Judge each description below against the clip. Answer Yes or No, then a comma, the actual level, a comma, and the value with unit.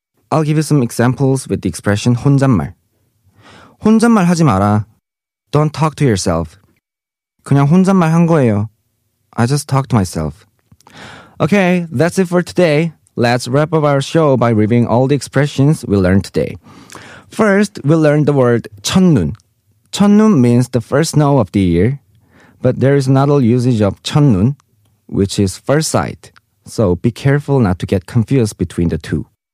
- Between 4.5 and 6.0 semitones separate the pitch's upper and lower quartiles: Yes, wide, 5.5 semitones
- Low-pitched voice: Yes, low, 125 Hz